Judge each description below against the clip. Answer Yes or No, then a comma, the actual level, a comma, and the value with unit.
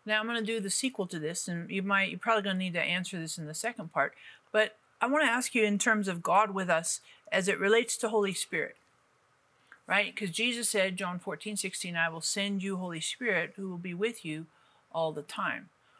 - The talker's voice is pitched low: No, high, 195 Hz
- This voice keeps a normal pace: No, fast, 230 wpm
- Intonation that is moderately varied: Yes, average, 3.5 semitones